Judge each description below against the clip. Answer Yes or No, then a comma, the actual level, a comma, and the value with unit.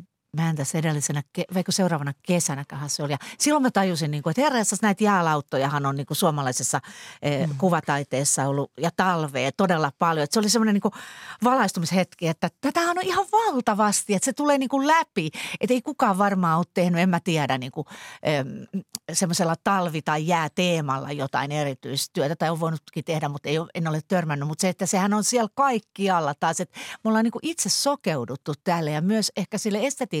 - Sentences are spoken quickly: Yes, fast, 160 wpm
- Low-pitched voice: No, medium, 175 Hz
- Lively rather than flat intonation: Yes, wide, 5.8 semitones